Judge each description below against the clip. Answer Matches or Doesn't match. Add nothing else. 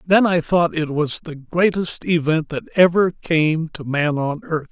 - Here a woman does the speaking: Doesn't match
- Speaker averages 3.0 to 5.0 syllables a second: Matches